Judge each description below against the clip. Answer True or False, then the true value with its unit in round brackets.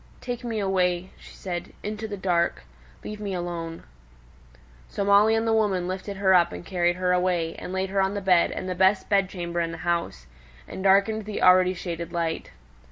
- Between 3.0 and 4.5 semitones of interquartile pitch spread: False (2.5 semitones)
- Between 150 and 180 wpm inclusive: False (200 wpm)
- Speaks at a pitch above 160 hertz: True (185 Hz)